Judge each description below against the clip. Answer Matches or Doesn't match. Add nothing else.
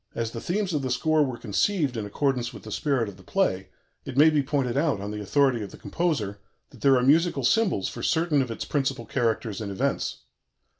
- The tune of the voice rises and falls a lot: Doesn't match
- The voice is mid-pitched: Doesn't match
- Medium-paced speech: Doesn't match